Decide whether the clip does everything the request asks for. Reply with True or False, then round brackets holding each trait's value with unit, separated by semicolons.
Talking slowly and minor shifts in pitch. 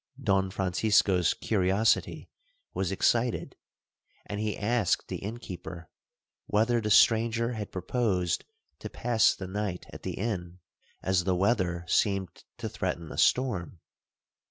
False (125 wpm; 3.6 semitones)